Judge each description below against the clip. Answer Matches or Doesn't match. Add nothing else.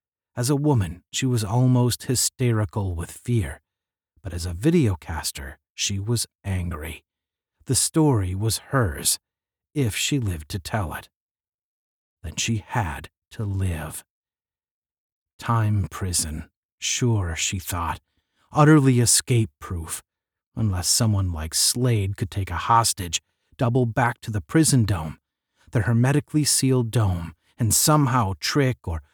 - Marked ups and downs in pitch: Matches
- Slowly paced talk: Matches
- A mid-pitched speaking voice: Doesn't match